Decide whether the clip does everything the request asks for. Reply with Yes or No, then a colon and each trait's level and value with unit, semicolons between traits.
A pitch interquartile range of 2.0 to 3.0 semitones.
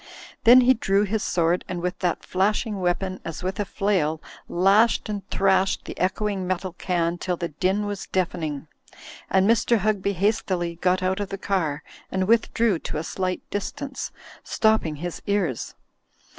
Yes: average, 2.7 semitones